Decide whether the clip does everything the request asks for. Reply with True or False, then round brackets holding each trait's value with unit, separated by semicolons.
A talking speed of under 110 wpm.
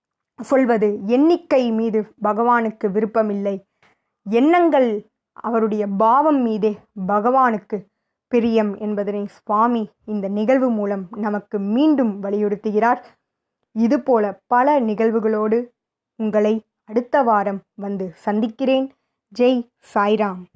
True (85 wpm)